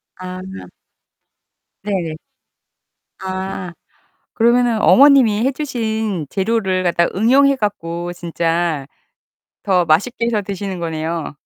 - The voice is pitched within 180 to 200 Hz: Yes, high, 190 Hz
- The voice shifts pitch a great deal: No, average, 4.9 semitones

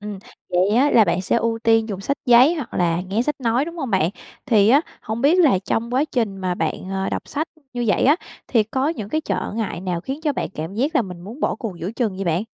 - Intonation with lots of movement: Yes, wide, 5.9 semitones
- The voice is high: Yes, high, 225 Hz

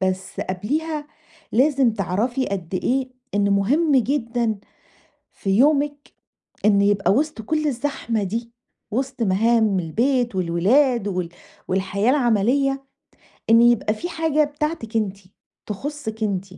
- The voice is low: No, high, 230 Hz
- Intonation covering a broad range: Yes, wide, 5.7 semitones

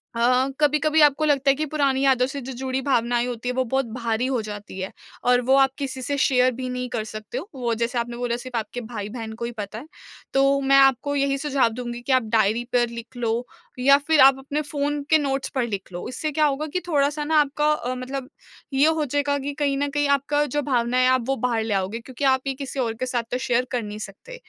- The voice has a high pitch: Yes, very high, 260 Hz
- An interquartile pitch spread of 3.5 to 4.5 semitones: No, average, 2.9 semitones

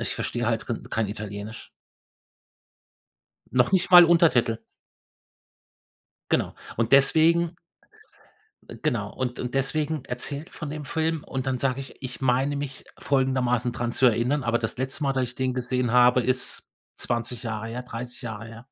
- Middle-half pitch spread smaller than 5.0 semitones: Yes, average, 2.9 semitones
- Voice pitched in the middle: No, low, 125 Hz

